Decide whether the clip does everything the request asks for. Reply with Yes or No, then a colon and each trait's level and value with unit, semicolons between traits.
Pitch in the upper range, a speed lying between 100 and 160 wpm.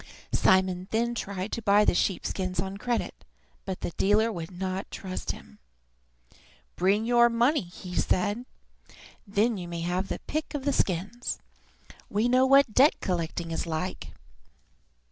Yes: high, 195 Hz; average, 150 wpm